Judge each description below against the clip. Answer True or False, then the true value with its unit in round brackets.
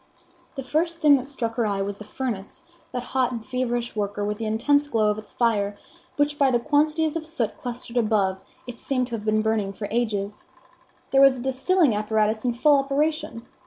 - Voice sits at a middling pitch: False (240 Hz)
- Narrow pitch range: False (4.3 semitones)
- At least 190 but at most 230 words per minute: True (200 wpm)